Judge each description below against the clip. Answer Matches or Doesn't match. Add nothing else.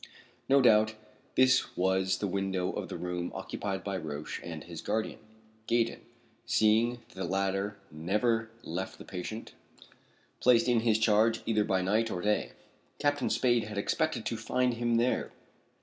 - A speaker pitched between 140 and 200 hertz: Doesn't match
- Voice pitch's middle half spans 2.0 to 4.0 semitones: Matches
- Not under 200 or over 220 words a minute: Doesn't match